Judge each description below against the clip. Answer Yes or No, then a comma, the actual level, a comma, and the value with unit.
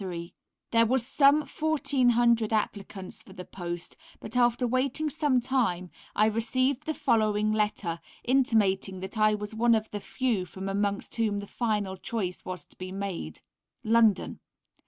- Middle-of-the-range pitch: No, high, 220 Hz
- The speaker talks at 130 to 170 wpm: Yes, average, 150 wpm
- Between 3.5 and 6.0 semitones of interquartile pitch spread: Yes, average, 4.0 semitones